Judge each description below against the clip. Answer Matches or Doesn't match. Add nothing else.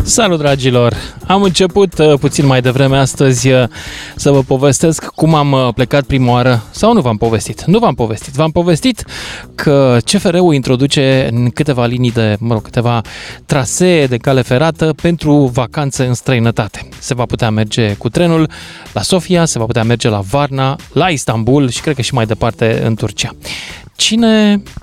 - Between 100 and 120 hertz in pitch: Doesn't match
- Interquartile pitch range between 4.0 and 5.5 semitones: Matches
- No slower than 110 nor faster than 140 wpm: Doesn't match